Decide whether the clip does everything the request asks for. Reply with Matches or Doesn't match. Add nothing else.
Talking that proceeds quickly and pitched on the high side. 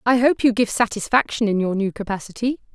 Doesn't match